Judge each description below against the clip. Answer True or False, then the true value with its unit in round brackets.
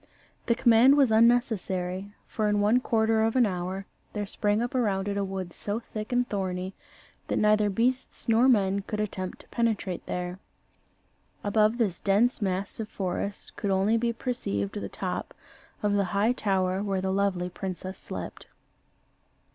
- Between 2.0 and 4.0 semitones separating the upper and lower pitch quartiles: True (3.1 semitones)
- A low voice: False (205 Hz)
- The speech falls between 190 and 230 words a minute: False (165 wpm)